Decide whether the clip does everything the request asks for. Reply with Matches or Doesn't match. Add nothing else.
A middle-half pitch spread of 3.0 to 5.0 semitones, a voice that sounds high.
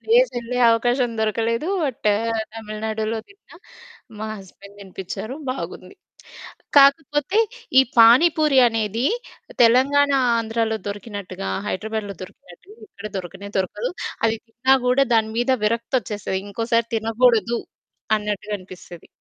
Matches